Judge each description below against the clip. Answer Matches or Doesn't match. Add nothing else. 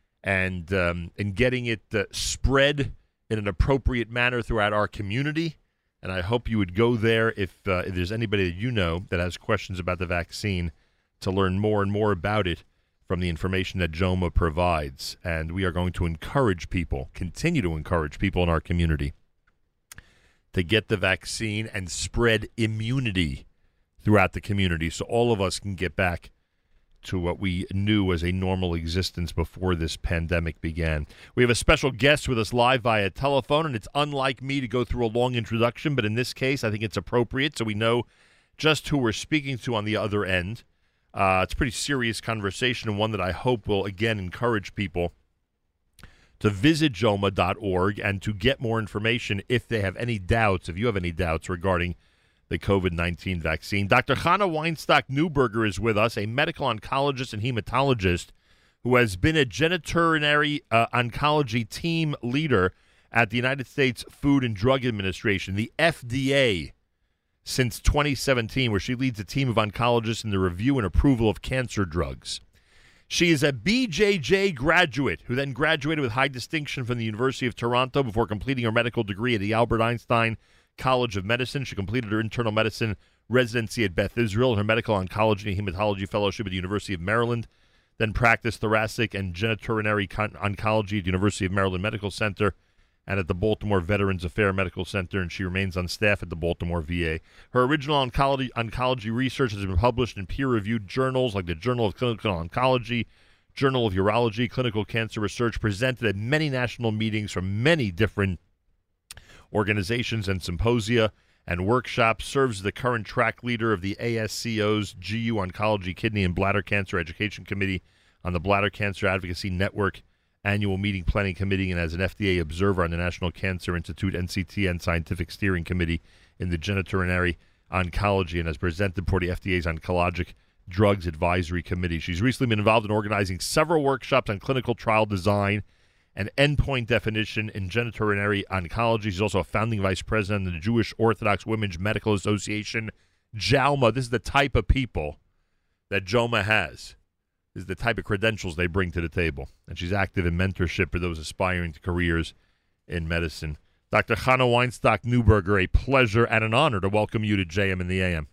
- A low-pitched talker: Matches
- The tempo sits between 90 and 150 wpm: Doesn't match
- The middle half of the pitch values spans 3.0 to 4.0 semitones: Doesn't match